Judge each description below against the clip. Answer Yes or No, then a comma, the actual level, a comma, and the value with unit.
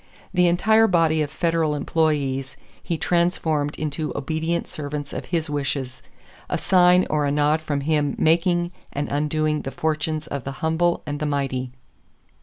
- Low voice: No, medium, 155 Hz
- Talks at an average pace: Yes, average, 155 wpm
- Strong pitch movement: No, narrow, 2.5 semitones